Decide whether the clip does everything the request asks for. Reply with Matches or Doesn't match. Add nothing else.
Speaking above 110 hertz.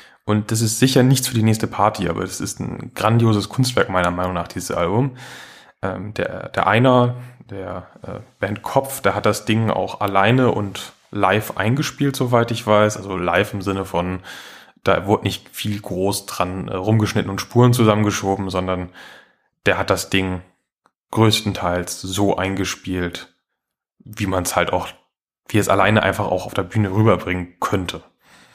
Doesn't match